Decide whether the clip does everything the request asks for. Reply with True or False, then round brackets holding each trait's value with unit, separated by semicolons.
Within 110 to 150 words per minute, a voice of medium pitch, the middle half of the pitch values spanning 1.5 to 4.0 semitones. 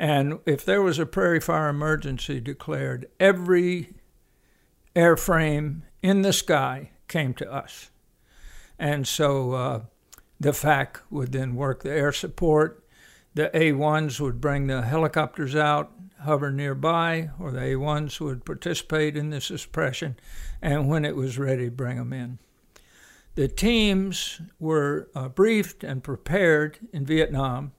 True (140 wpm; 150 Hz; 3.3 semitones)